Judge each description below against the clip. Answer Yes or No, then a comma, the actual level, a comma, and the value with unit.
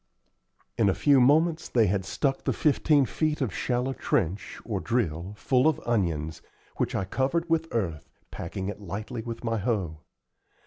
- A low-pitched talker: Yes, low, 115 Hz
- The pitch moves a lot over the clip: Yes, wide, 6.1 semitones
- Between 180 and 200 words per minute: No, average, 165 wpm